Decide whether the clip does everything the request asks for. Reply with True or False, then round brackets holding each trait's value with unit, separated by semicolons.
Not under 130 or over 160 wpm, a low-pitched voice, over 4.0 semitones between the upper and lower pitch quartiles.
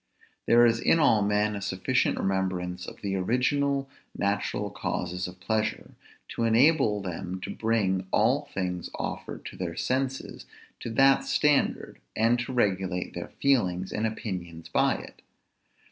True (145 wpm; 105 Hz; 4.6 semitones)